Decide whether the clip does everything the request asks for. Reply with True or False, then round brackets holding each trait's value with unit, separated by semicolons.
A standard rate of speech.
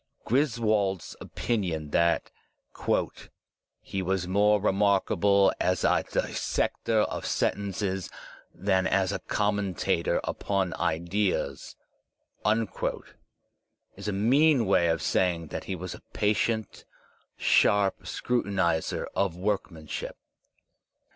False (95 wpm)